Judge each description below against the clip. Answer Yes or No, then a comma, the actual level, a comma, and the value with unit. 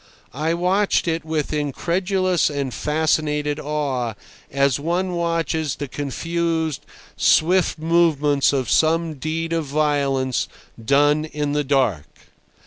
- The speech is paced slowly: Yes, slow, 115 wpm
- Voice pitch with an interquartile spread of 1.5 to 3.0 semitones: Yes, average, 2.7 semitones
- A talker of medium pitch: Yes, medium, 150 Hz